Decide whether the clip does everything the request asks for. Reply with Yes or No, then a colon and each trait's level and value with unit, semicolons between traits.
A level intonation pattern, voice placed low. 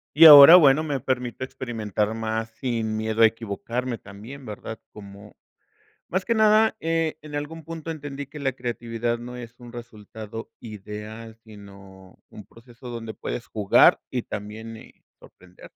No: average, 4.1 semitones; low, 115 Hz